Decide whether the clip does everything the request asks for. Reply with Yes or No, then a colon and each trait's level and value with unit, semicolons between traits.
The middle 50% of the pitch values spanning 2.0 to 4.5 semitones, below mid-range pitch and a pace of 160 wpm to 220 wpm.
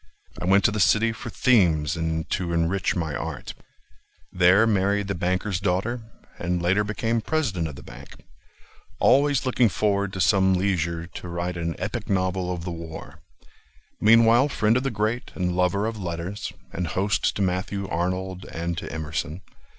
Yes: average, 3.7 semitones; very low, 95 Hz; average, 165 wpm